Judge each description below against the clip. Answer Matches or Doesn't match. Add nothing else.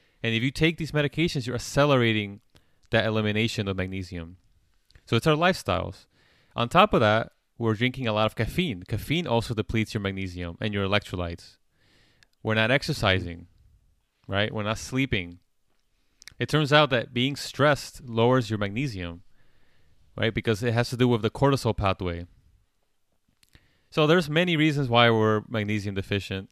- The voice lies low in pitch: Matches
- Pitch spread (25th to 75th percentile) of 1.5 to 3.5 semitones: Doesn't match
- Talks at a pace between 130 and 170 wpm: Matches